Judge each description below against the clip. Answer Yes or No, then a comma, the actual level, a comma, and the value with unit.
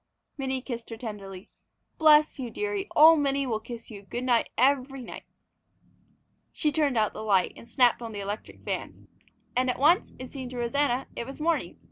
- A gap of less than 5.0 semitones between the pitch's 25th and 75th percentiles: Yes, average, 3.7 semitones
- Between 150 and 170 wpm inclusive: No, average, 185 wpm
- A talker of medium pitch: No, very high, 255 Hz